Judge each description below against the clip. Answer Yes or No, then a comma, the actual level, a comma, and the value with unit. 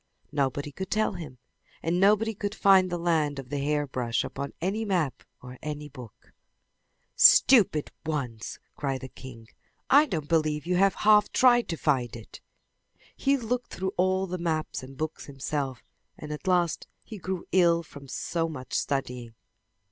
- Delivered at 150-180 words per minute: Yes, average, 165 wpm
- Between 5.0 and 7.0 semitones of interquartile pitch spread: Yes, wide, 5.5 semitones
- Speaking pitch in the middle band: Yes, medium, 155 Hz